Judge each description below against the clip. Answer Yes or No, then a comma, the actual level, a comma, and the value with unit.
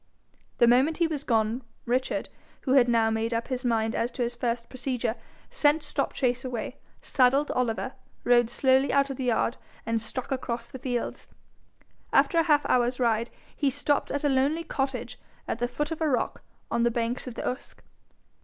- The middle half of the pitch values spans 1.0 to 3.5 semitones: Yes, narrow, 2.6 semitones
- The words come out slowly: No, average, 185 wpm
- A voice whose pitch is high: Yes, very high, 250 Hz